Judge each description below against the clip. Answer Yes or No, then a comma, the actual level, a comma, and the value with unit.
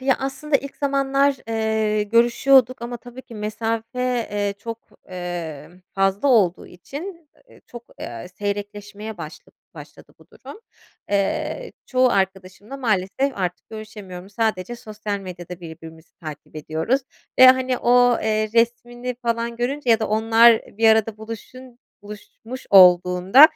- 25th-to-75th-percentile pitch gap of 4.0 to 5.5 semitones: Yes, average, 4.4 semitones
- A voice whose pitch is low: No, high, 220 Hz